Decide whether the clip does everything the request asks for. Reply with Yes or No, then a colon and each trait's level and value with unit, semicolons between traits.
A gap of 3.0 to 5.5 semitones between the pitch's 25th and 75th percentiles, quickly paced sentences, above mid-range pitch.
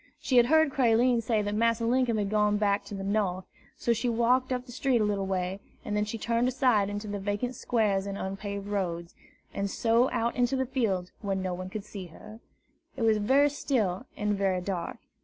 Yes: average, 3.4 semitones; fast, 215 wpm; high, 210 Hz